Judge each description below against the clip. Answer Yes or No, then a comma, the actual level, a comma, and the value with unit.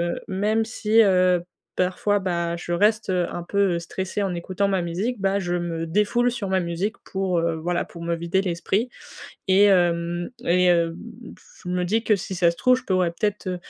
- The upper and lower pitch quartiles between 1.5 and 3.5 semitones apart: Yes, average, 2.9 semitones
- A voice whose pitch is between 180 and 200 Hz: Yes, medium, 185 Hz